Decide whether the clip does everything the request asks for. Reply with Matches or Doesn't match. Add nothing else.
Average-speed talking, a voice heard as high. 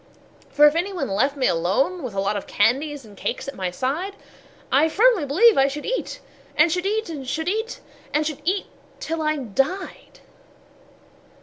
Matches